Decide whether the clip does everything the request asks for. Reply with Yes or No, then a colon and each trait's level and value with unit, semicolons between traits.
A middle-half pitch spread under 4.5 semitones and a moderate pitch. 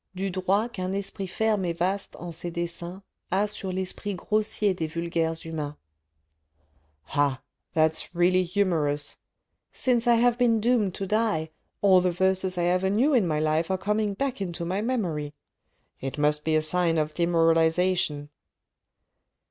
Yes: average, 3.8 semitones; medium, 180 Hz